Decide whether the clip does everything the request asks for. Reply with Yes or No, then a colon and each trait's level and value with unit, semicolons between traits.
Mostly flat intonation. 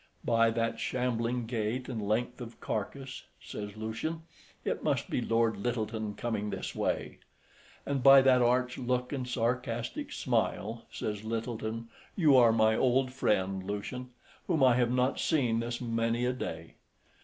Yes: narrow, 2.3 semitones